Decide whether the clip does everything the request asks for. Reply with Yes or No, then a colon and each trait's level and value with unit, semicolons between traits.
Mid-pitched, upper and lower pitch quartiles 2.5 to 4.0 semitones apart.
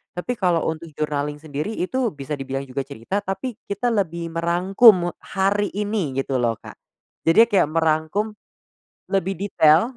No: medium, 170 Hz; average, 5.2 semitones